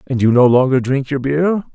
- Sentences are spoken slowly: No, fast, 240 wpm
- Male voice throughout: Yes, male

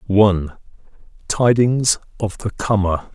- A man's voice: Yes, male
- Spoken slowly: Yes, slow, 75 wpm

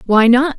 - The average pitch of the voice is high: Yes, very high, 250 Hz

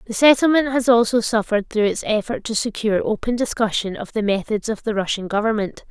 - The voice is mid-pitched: No, high, 220 Hz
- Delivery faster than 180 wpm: Yes, average, 195 wpm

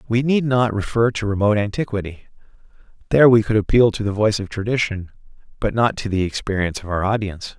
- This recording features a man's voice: Yes, male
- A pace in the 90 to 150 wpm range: No, average, 190 wpm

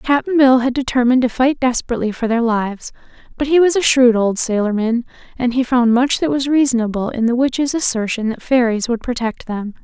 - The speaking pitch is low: No, high, 245 Hz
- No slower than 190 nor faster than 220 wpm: Yes, average, 200 wpm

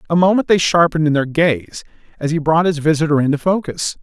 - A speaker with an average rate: No, fast, 210 wpm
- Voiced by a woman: No, male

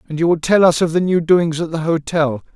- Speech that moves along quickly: Yes, fast, 280 wpm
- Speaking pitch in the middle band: Yes, medium, 165 Hz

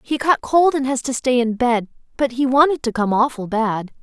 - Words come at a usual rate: No, fast, 240 wpm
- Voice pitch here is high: Yes, very high, 250 Hz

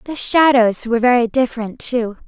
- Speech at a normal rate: Yes, average, 160 wpm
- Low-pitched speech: No, high, 240 Hz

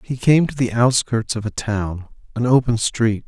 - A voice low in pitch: Yes, low, 115 Hz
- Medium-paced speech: Yes, average, 185 wpm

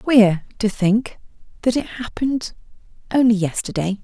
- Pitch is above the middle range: Yes, high, 220 Hz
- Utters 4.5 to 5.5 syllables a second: Yes, 4.6 syllables/s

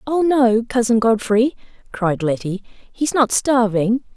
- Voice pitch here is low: No, high, 235 Hz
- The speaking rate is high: No, average, 145 wpm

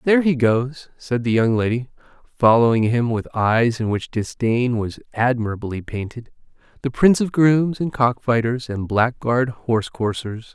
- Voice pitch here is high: No, low, 120 Hz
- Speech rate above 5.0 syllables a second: No, 4.6 syllables/s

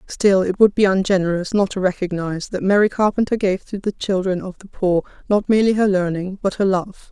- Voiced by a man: No, female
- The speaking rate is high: Yes, fast, 210 wpm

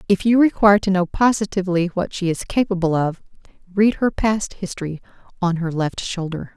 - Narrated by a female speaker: Yes, female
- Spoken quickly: No, average, 175 wpm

